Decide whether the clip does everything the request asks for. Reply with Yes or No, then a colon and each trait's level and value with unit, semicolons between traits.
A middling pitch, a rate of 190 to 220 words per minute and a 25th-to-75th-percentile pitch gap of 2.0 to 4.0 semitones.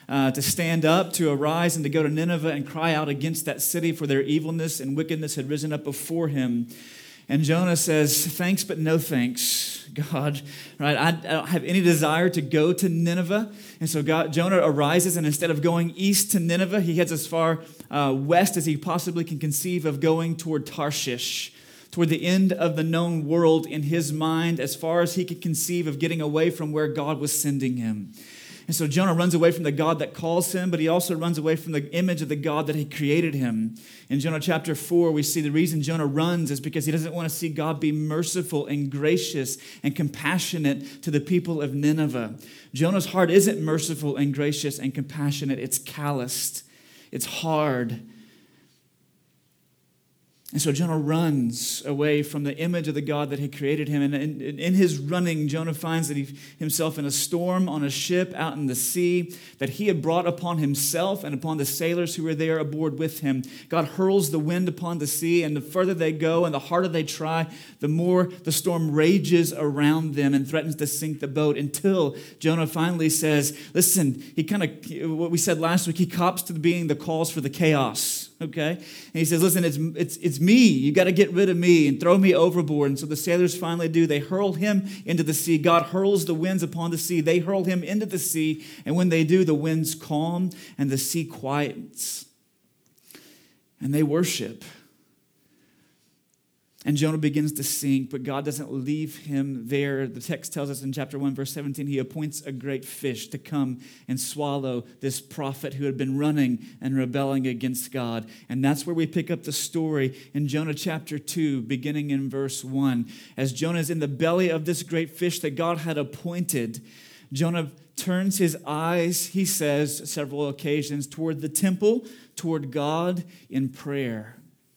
Yes: medium, 155 Hz; average, 200 wpm; average, 2.9 semitones